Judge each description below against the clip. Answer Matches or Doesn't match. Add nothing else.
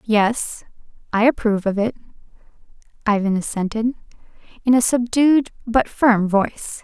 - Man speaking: Doesn't match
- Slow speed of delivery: Matches